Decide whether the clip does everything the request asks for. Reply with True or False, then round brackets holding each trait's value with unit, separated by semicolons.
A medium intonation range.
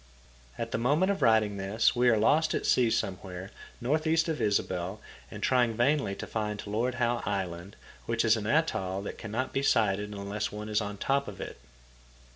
True (3.9 semitones)